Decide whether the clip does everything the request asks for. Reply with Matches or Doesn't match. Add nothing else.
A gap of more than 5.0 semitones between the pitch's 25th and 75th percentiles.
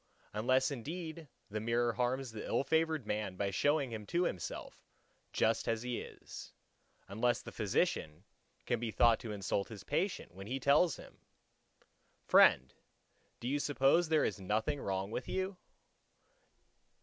Matches